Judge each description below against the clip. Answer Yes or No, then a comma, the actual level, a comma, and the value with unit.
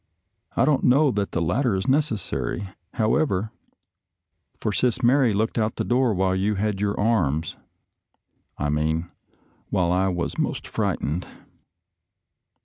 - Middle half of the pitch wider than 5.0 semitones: Yes, wide, 5.4 semitones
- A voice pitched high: No, low, 100 Hz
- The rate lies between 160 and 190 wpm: No, average, 145 wpm